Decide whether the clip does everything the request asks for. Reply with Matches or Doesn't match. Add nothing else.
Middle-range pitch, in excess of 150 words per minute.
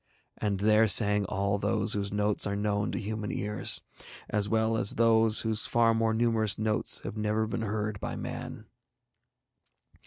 Doesn't match